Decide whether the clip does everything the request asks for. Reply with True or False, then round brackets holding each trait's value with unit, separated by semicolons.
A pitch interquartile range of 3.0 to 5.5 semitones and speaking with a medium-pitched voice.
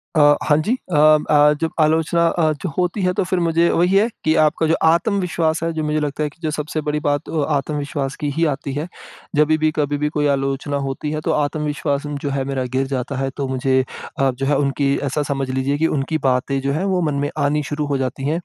False (2.4 semitones; 150 Hz)